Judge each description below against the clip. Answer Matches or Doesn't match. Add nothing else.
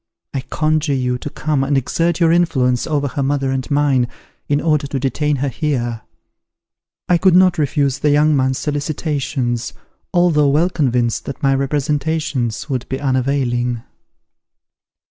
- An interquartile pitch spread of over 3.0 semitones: Doesn't match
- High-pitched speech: Doesn't match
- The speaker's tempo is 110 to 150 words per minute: Matches